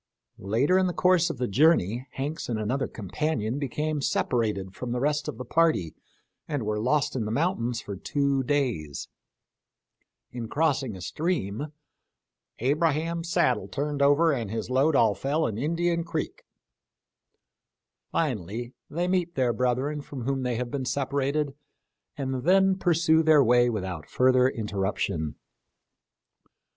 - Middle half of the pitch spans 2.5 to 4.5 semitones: No, average, 5.1 semitones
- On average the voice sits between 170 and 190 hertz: No, low, 135 Hz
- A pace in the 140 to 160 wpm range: Yes, average, 145 wpm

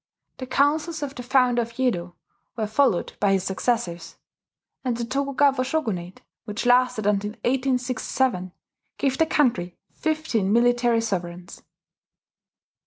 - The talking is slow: Yes, slow, 120 wpm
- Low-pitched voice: No, high, 245 Hz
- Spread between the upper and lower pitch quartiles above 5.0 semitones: No, average, 4.6 semitones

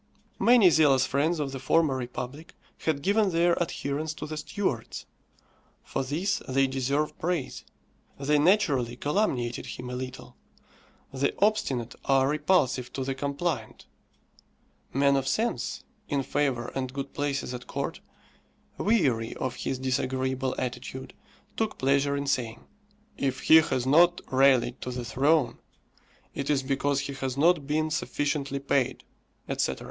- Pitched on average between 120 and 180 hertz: Yes, medium, 140 Hz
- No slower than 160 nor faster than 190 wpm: No, average, 140 wpm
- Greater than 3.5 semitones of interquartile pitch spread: No, average, 3.0 semitones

